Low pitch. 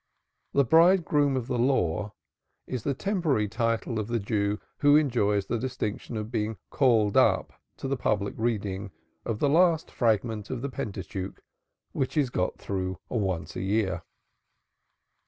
Yes: low, 115 Hz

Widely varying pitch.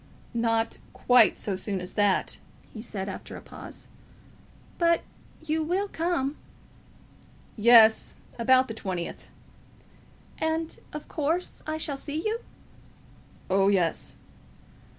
Yes: wide, 7.6 semitones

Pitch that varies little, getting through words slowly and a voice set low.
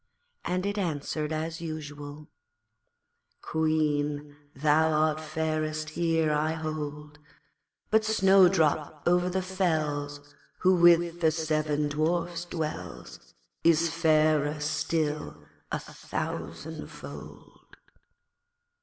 No: narrow, 2.0 semitones; slow, 90 wpm; medium, 155 Hz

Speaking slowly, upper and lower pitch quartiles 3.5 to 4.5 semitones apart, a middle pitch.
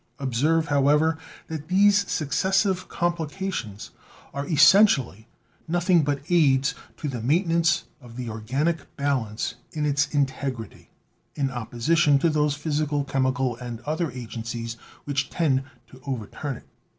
Yes: slow, 125 wpm; average, 4.2 semitones; medium, 145 Hz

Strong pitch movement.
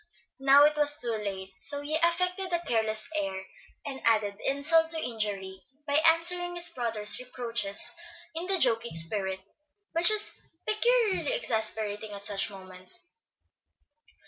Yes: wide, 8.3 semitones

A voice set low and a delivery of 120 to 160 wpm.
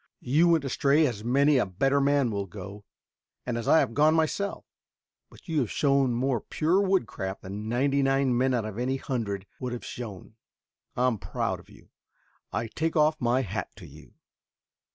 No: low, 130 Hz; average, 180 wpm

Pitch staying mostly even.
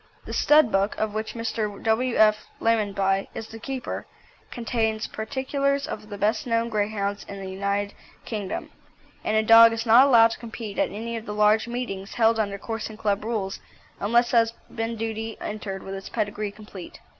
Yes: narrow, 2.0 semitones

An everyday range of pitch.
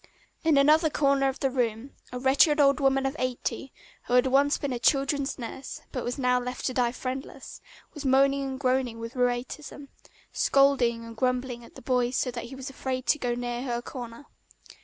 No: narrow, 2.0 semitones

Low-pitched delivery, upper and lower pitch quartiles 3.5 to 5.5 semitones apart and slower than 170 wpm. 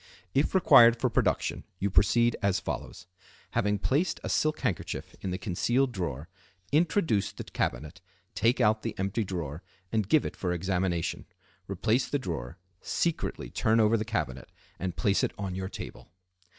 Yes: low, 100 Hz; average, 4.6 semitones; average, 155 wpm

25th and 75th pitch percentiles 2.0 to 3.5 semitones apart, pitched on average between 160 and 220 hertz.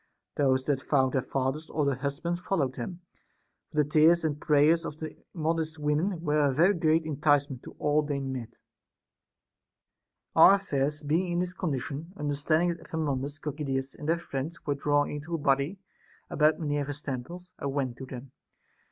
No: average, 2.7 semitones; medium, 150 Hz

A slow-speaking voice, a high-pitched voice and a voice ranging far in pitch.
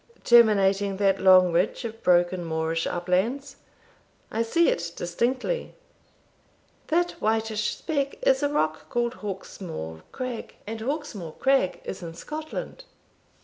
Yes: slow, 120 wpm; high, 210 Hz; wide, 6.4 semitones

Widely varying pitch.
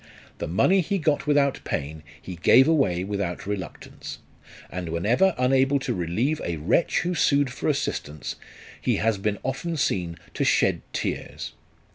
Yes: wide, 8.6 semitones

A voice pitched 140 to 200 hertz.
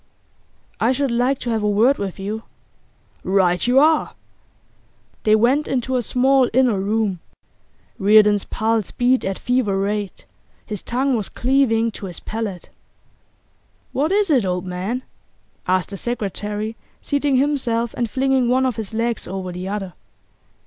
No: high, 225 Hz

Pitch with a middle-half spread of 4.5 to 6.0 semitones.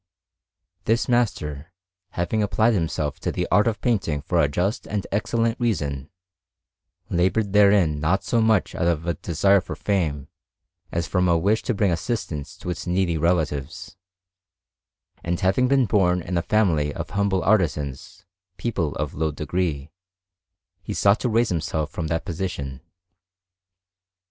Yes: average, 4.8 semitones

